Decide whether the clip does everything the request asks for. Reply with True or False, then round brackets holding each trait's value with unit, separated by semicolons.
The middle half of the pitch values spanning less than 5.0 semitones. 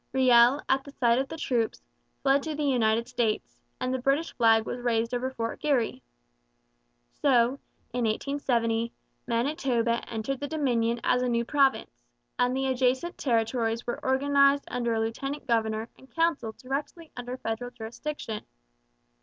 True (3.0 semitones)